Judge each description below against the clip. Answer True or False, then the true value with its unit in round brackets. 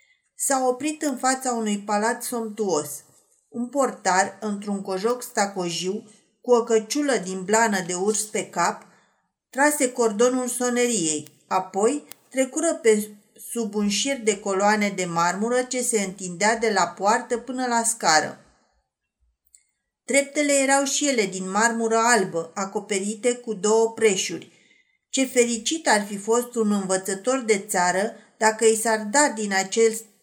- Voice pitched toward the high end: True (225 Hz)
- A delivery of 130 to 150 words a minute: True (135 wpm)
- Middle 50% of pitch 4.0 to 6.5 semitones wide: False (3.5 semitones)